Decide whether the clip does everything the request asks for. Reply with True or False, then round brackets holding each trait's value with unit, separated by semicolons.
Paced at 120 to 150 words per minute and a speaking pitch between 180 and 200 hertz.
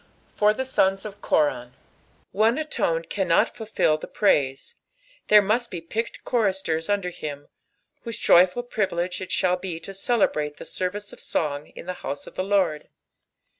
False (160 wpm; 185 Hz)